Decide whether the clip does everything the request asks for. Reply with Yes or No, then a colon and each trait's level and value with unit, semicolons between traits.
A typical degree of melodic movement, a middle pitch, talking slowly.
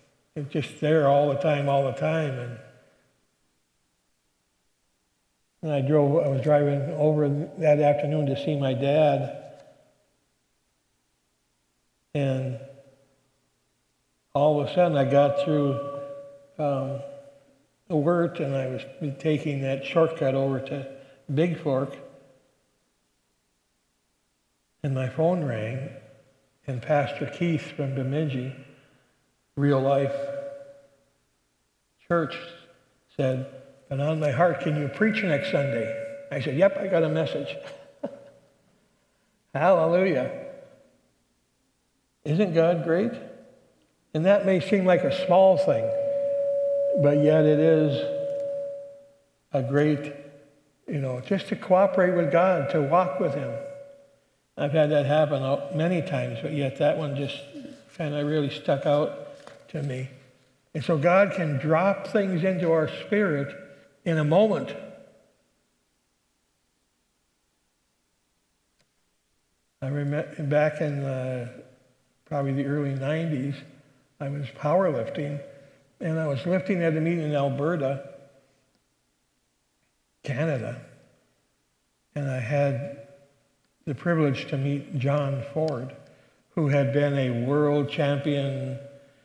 Yes: average, 3.8 semitones; medium, 145 Hz; slow, 115 wpm